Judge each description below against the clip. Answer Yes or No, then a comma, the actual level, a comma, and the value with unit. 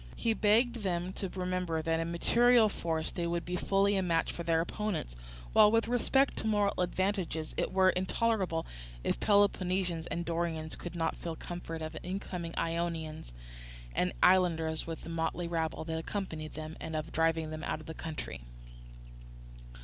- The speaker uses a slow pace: No, average, 165 wpm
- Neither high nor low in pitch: Yes, medium, 170 Hz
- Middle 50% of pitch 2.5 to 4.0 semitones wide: Yes, average, 3.0 semitones